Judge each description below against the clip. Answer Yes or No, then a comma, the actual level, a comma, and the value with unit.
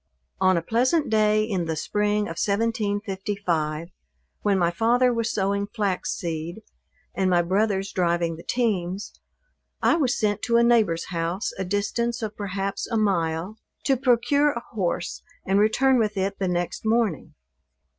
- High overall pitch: Yes, high, 205 Hz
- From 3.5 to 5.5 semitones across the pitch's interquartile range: Yes, average, 4.1 semitones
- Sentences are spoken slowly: No, average, 155 wpm